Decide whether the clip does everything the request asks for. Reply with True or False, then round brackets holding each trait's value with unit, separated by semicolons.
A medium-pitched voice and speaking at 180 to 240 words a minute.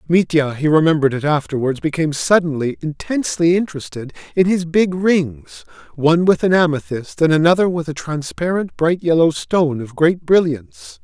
False (155 Hz; 150 wpm)